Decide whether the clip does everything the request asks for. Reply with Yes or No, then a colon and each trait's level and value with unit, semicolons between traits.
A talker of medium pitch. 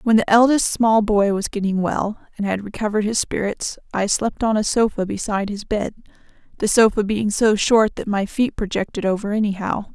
No: high, 210 Hz